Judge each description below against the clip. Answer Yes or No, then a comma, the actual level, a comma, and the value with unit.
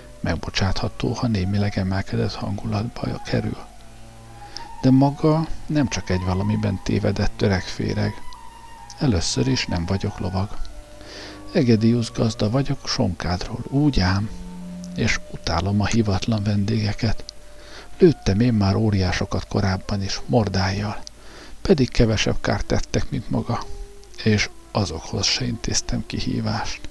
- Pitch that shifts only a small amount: No, average, 3.2 semitones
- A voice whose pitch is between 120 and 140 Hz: No, low, 105 Hz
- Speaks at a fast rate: No, slow, 105 wpm